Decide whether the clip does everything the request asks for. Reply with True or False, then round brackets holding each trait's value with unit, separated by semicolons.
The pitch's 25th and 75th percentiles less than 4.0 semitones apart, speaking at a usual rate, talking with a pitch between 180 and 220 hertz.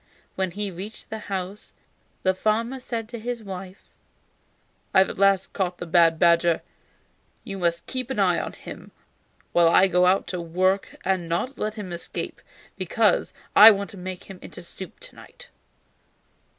True (3.1 semitones; 170 wpm; 190 Hz)